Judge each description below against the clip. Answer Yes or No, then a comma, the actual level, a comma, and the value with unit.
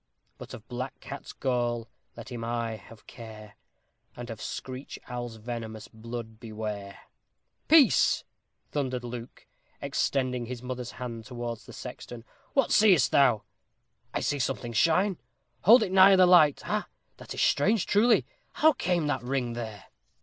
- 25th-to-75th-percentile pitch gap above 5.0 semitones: No, average, 4.0 semitones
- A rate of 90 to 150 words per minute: Yes, average, 145 wpm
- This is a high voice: No, low, 120 Hz